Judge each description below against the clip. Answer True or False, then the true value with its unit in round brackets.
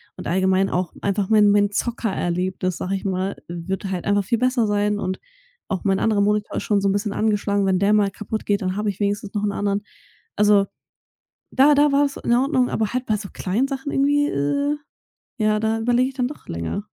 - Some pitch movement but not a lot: True (3.1 semitones)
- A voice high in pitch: True (205 Hz)